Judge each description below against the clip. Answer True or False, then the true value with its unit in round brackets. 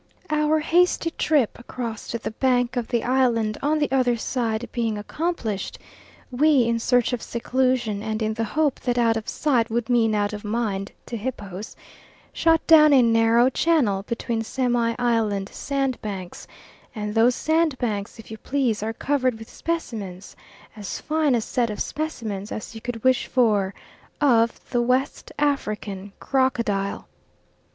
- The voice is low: False (235 Hz)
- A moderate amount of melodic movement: True (3.4 semitones)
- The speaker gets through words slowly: False (155 wpm)